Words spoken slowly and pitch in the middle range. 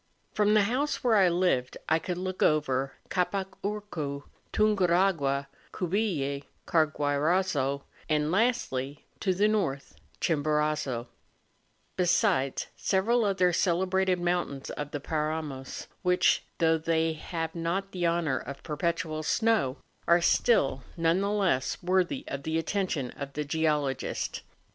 Yes: slow, 125 wpm; medium, 170 Hz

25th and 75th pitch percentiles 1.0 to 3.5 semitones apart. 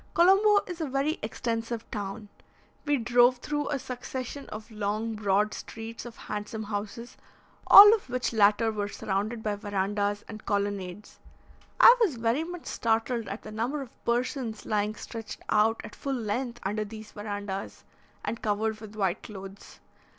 Yes: average, 3.1 semitones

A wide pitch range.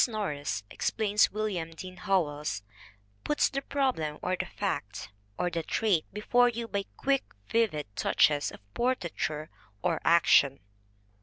Yes: wide, 6.5 semitones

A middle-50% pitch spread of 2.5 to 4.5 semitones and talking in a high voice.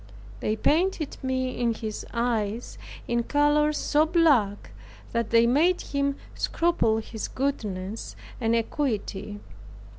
No: average, 5.1 semitones; high, 240 Hz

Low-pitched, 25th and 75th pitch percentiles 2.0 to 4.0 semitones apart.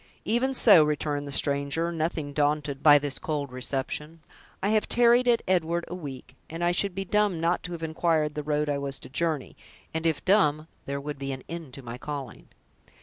No: medium, 155 Hz; average, 3.4 semitones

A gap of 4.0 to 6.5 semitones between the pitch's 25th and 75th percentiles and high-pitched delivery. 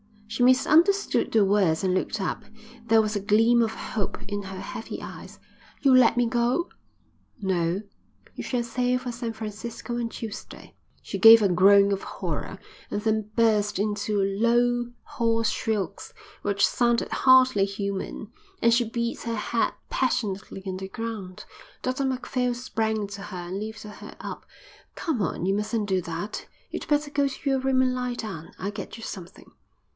No: average, 3.3 semitones; high, 220 Hz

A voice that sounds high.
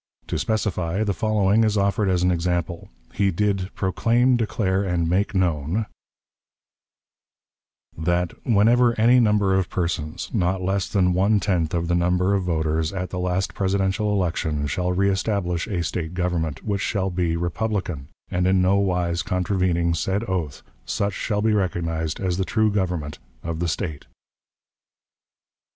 No: very low, 95 Hz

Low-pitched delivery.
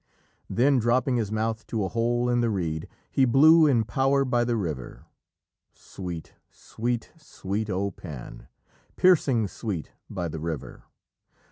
Yes: low, 115 Hz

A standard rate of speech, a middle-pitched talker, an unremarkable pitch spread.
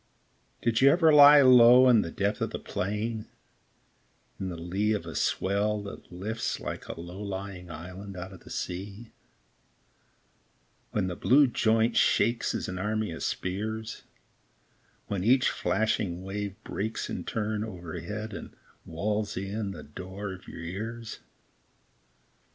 No: average, 145 wpm; low, 105 Hz; average, 3.2 semitones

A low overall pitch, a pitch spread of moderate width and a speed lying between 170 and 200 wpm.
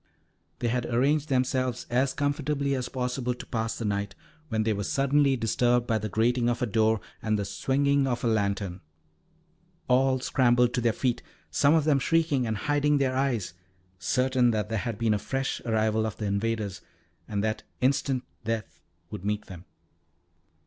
Yes: low, 120 Hz; average, 3.4 semitones; average, 175 wpm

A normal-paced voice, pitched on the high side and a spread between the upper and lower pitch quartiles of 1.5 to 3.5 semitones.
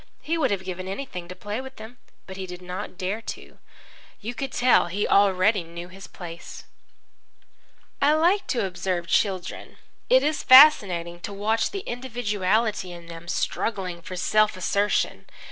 No: average, 160 wpm; high, 200 Hz; average, 4.8 semitones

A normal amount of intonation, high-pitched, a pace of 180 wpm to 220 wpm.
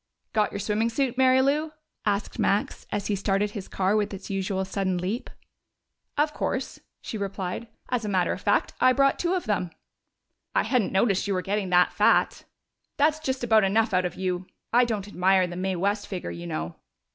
Yes: average, 3.8 semitones; high, 200 Hz; average, 195 wpm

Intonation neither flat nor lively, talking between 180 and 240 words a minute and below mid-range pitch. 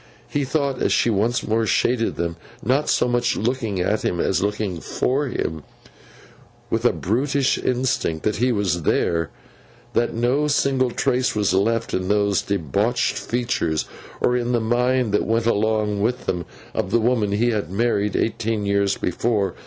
No: average, 3.5 semitones; average, 160 wpm; low, 115 Hz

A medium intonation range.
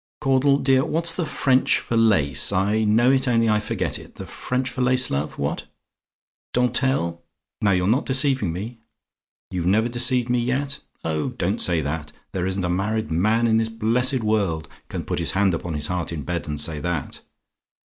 No: wide, 6.3 semitones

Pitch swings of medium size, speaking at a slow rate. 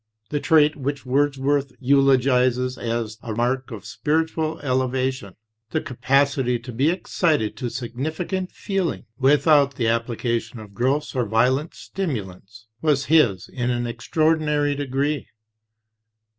Yes: average, 3.7 semitones; slow, 120 wpm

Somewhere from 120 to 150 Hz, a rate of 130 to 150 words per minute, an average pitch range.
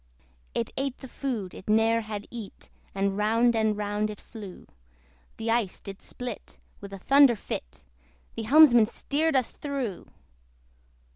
No: high, 225 Hz; average, 145 wpm; average, 3.3 semitones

